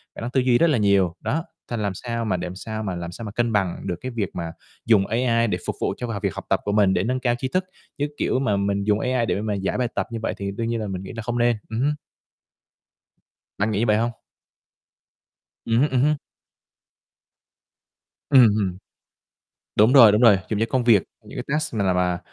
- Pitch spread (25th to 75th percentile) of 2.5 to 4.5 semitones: Yes, average, 3.4 semitones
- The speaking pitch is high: No, low, 110 Hz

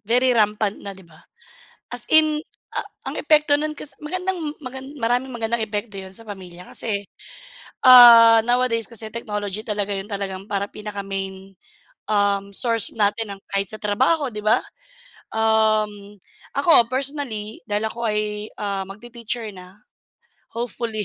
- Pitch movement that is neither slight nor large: Yes, average, 3.1 semitones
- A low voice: No, high, 215 Hz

